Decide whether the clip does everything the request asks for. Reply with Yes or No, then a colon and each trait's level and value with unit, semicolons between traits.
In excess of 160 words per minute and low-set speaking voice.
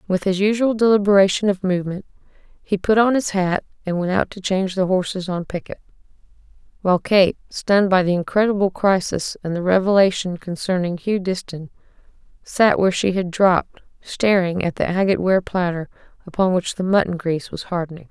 No: average, 170 wpm; high, 190 Hz